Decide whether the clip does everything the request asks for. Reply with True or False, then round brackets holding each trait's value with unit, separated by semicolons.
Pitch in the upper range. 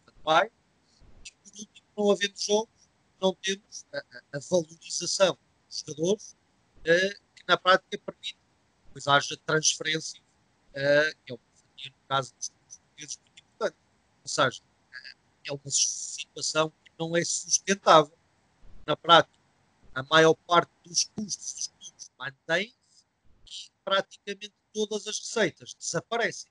False (165 Hz)